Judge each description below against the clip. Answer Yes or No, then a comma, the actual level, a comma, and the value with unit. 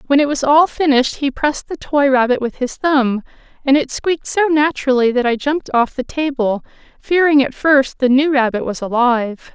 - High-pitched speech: Yes, very high, 270 Hz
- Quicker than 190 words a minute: Yes, average, 200 wpm